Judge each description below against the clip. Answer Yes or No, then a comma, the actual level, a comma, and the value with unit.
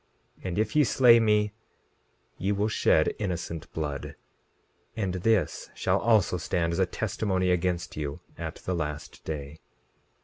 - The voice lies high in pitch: No, very low, 90 Hz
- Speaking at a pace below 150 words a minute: Yes, average, 140 wpm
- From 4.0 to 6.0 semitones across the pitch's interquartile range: Yes, average, 4.3 semitones